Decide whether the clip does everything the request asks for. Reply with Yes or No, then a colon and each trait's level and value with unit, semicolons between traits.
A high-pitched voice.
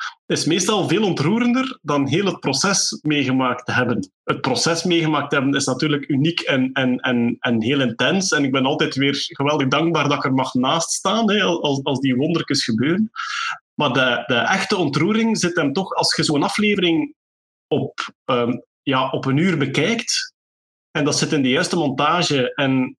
No: medium, 145 Hz